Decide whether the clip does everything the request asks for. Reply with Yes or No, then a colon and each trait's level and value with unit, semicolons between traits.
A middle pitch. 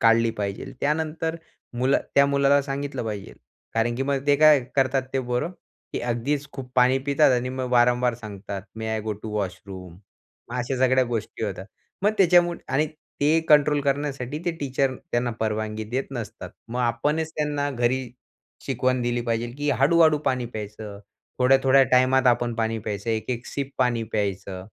No: low, 125 Hz